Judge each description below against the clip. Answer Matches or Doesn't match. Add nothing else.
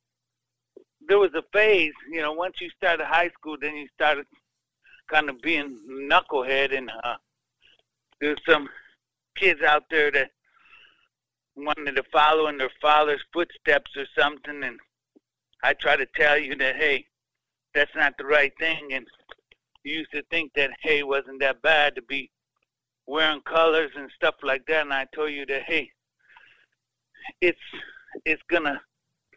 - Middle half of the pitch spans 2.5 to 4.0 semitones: Matches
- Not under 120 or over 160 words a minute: Matches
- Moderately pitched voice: Matches